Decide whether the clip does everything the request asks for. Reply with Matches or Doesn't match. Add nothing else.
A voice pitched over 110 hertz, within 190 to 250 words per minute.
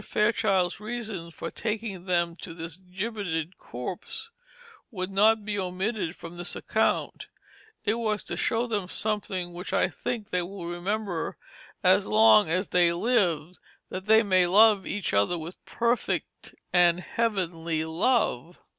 Doesn't match